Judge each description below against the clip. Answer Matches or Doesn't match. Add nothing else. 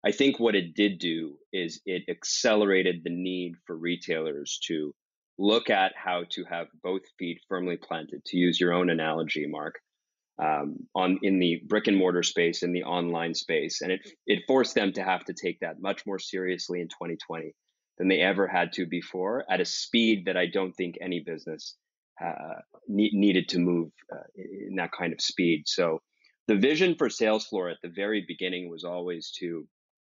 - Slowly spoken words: Doesn't match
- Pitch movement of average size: Doesn't match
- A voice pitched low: Matches